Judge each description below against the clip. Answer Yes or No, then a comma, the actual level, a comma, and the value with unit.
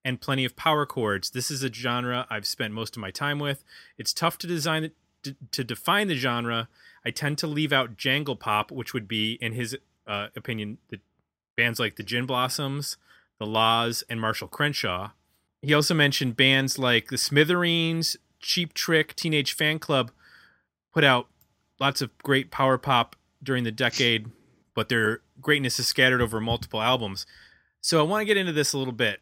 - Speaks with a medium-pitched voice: No, low, 130 Hz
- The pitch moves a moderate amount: Yes, average, 4.1 semitones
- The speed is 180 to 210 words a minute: Yes, average, 185 wpm